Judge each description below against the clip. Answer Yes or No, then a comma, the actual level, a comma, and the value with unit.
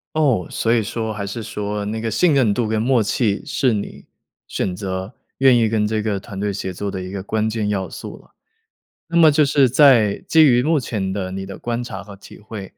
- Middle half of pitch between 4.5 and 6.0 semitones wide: No, average, 3.5 semitones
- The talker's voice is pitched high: No, low, 110 Hz